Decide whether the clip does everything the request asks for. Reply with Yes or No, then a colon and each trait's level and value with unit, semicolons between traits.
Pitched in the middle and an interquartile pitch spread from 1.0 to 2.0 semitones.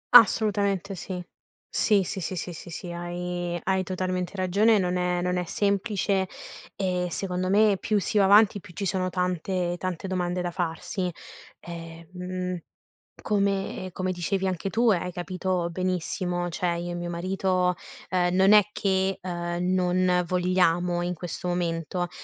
Yes: medium, 180 Hz; narrow, 1.5 semitones